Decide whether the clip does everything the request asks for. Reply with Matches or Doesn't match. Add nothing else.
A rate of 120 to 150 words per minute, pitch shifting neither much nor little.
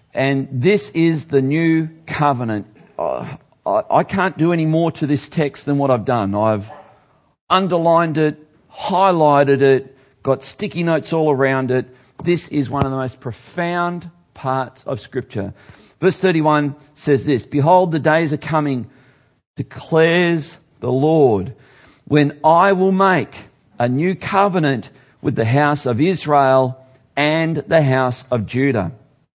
Matches